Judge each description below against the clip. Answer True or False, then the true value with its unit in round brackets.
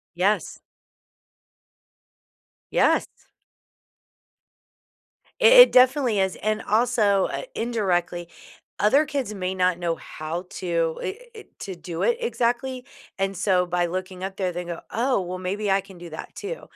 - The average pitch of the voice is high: True (195 Hz)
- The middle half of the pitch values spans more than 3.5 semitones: True (5.2 semitones)